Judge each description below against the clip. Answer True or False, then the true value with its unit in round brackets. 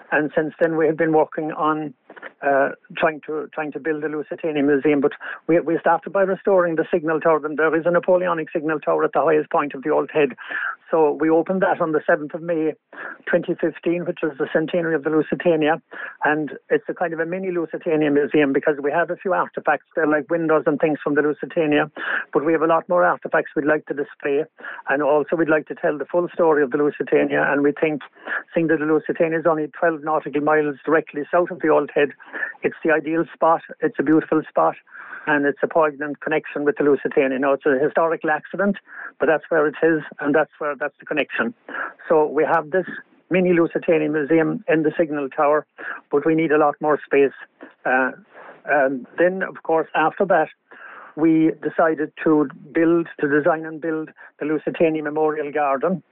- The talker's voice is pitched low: False (155 Hz)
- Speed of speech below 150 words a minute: False (205 wpm)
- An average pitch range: False (1.8 semitones)